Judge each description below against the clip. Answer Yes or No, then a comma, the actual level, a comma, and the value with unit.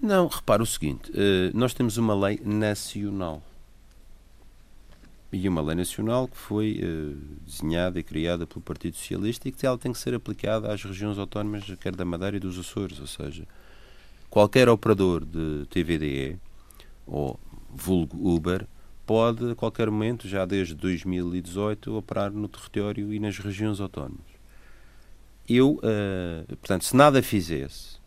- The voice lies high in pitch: No, low, 100 Hz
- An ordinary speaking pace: Yes, average, 145 wpm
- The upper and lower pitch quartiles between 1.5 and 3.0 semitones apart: No, average, 3.7 semitones